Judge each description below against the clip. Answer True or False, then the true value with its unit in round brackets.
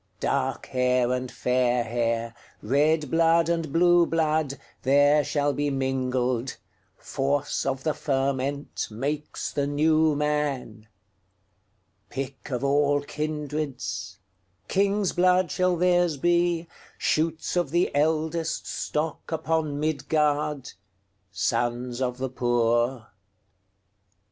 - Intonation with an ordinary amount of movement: True (4.4 semitones)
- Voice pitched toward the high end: False (140 Hz)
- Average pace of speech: False (80 wpm)